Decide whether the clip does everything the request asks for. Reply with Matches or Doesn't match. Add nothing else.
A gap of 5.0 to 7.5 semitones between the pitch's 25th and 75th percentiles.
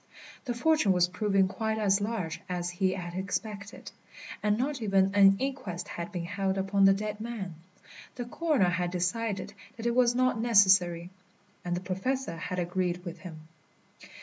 Doesn't match